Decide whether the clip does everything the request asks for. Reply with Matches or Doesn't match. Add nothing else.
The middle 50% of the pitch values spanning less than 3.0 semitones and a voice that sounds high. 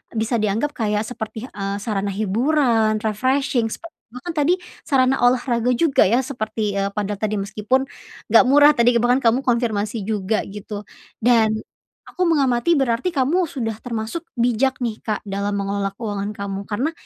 Doesn't match